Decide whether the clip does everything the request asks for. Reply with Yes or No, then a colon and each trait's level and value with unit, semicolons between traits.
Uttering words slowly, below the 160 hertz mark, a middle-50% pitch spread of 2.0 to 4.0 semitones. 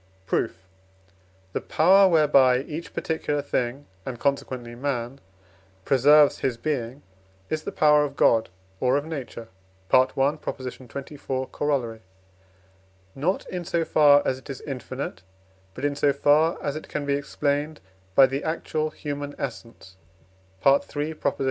Yes: slow, 130 wpm; medium, 140 Hz; narrow, 2.6 semitones